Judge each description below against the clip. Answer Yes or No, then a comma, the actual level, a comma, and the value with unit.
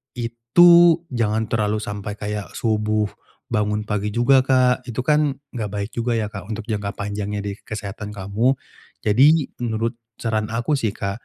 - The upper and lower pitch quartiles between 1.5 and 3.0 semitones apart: Yes, average, 2.7 semitones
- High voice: No, low, 110 Hz